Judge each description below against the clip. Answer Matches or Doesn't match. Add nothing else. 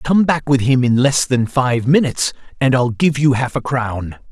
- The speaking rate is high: Matches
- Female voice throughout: Doesn't match